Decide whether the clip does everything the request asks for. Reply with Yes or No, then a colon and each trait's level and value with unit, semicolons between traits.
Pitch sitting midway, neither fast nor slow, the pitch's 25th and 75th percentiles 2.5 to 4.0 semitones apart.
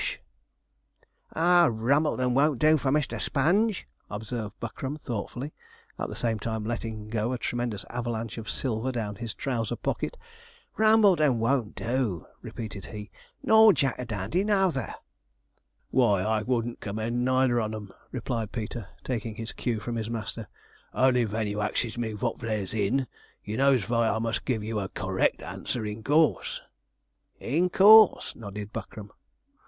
No: low, 115 Hz; average, 150 wpm; average, 3.6 semitones